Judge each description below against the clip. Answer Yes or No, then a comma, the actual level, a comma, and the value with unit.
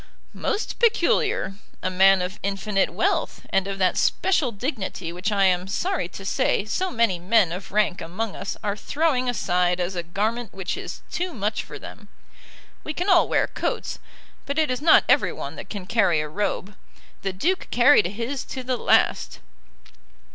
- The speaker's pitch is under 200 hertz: No, high, 205 Hz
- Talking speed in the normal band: Yes, average, 175 wpm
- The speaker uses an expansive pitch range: Yes, wide, 5.9 semitones